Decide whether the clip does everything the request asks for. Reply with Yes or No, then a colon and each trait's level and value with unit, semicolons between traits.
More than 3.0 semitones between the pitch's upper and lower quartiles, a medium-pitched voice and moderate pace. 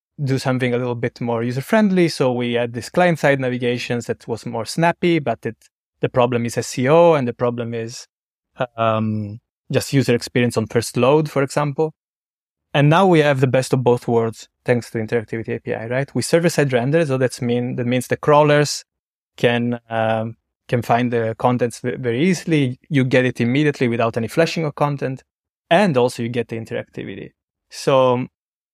No: average, 3.5 semitones; low, 125 Hz; average, 185 wpm